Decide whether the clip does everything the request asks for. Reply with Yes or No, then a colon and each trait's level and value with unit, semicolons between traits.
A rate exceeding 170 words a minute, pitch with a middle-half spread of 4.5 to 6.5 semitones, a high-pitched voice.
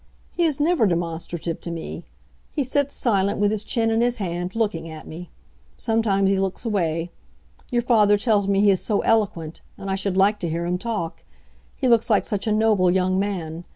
No: average, 200 wpm; average, 4.1 semitones; high, 200 Hz